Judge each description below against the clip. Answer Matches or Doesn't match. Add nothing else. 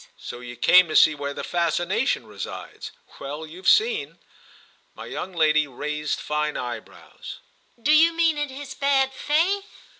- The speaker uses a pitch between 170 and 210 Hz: Matches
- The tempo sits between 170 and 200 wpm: Doesn't match